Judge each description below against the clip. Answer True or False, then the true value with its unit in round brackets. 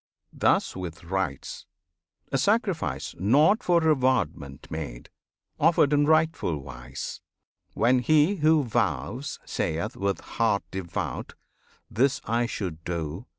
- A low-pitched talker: True (110 Hz)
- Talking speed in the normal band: False (110 wpm)